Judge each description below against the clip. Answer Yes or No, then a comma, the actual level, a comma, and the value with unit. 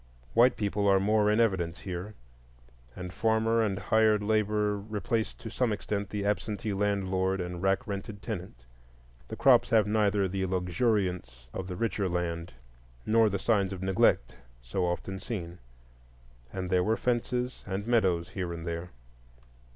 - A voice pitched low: Yes, low, 100 Hz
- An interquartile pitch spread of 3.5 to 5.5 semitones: No, average, 3.0 semitones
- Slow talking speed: No, average, 150 wpm